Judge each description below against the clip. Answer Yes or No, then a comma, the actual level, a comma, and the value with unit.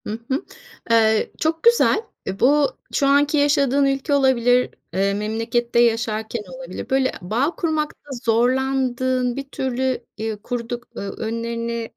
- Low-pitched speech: No, high, 245 Hz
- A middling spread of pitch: Yes, average, 3.2 semitones